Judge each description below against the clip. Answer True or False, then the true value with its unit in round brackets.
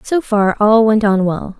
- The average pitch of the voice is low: False (215 Hz)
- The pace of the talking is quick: True (225 wpm)